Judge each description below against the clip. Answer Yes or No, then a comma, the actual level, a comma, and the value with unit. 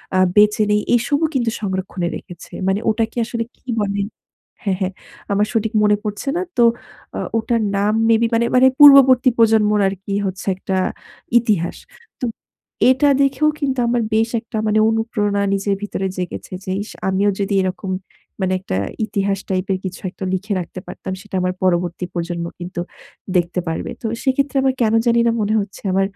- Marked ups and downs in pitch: No, average, 3.6 semitones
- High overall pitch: Yes, high, 205 Hz